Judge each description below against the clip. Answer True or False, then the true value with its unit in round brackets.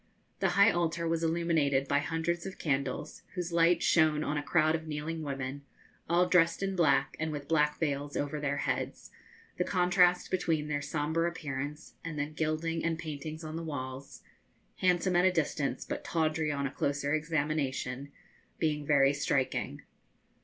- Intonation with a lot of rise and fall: False (2.6 semitones)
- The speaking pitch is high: False (155 Hz)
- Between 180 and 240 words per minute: False (165 wpm)